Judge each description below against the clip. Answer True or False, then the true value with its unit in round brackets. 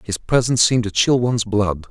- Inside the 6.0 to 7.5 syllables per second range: True (6.2 syllables/s)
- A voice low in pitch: True (110 Hz)